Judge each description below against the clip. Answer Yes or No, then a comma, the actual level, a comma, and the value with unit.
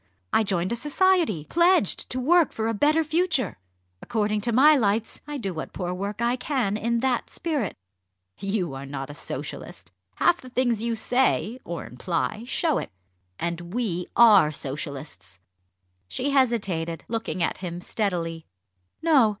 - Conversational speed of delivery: Yes, average, 155 wpm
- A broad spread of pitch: Yes, wide, 6.9 semitones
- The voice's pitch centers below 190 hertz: No, high, 220 Hz